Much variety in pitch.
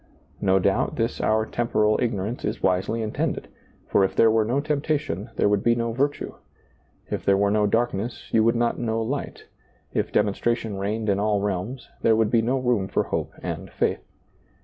No: average, 2.7 semitones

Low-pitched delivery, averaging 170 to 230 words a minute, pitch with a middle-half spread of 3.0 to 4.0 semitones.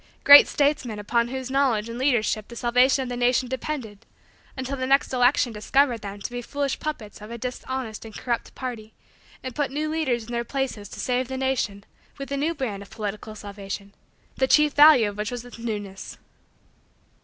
No: high, 245 Hz; average, 190 wpm; average, 3.7 semitones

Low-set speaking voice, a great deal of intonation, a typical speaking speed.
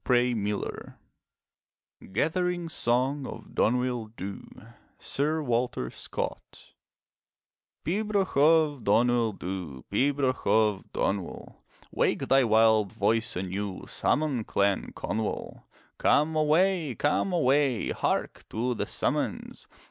No: low, 125 Hz; wide, 5.8 semitones; slow, 95 wpm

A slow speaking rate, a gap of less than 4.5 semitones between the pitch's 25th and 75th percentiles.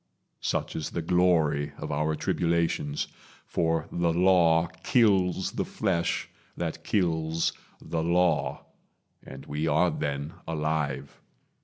Yes: slow, 115 wpm; narrow, 2.4 semitones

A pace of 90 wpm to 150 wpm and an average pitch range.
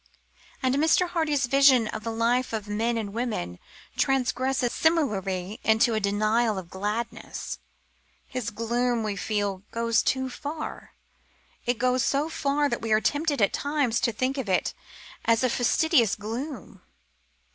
Yes: average, 145 wpm; average, 3.9 semitones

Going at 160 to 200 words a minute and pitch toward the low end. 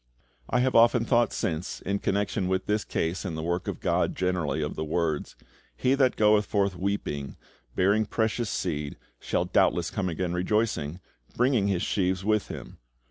Yes: average, 170 wpm; very low, 95 Hz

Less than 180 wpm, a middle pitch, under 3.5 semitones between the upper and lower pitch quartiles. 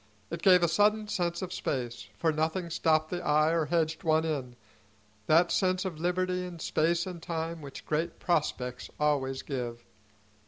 Yes: average, 165 wpm; medium, 165 Hz; average, 2.7 semitones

